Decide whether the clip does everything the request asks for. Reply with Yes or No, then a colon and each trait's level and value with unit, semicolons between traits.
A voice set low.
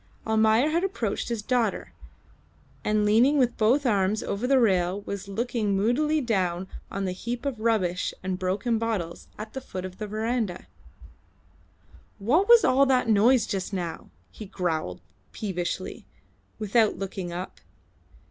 No: high, 215 Hz